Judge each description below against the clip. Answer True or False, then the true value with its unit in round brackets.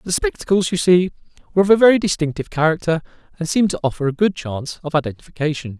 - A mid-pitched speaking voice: True (170 Hz)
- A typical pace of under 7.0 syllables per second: False (7.4 syllables/s)